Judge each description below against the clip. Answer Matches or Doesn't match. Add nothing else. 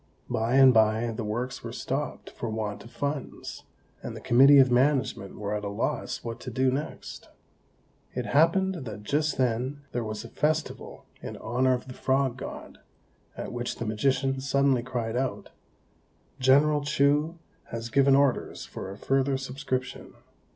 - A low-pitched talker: Matches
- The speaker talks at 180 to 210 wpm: Doesn't match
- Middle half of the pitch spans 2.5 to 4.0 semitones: Matches